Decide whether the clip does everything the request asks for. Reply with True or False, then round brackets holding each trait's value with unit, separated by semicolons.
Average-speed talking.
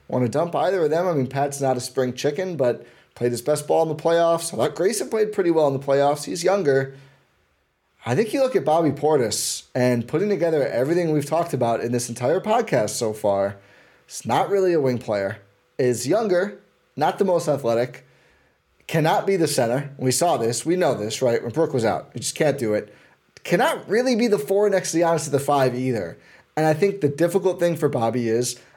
False (220 wpm)